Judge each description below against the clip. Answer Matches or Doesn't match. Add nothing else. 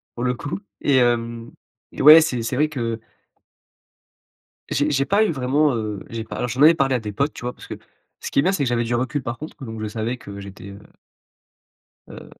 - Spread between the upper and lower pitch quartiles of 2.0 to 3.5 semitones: Doesn't match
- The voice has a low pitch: Matches